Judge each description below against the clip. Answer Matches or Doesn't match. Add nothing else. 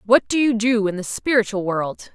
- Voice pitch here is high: Matches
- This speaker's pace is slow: Doesn't match